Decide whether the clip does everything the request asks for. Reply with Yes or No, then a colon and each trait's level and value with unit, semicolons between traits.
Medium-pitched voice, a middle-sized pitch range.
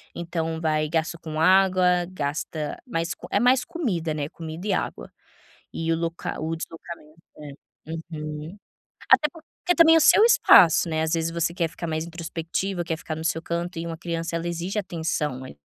No: medium, 165 Hz; narrow, 1.8 semitones